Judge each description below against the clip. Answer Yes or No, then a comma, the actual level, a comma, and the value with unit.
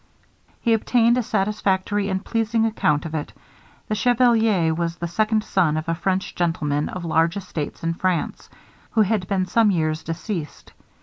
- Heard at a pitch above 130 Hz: Yes, high, 190 Hz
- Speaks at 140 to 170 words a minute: Yes, average, 165 wpm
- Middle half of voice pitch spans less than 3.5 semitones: No, average, 4.8 semitones